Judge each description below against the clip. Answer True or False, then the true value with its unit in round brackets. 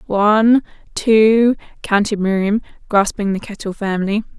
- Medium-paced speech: False (110 wpm)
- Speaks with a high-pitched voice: True (210 Hz)